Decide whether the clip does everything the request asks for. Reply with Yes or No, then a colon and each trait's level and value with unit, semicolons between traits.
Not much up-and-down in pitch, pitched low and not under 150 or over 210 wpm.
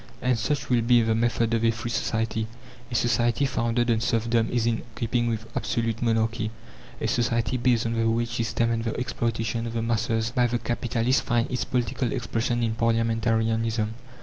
Yes: narrow, 0.9 semitones; low, 115 Hz; average, 180 wpm